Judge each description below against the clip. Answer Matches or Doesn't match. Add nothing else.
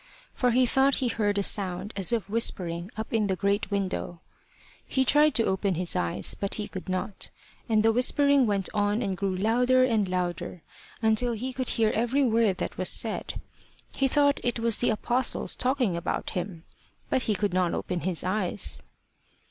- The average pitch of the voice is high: Matches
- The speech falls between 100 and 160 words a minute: Doesn't match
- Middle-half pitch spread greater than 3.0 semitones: Matches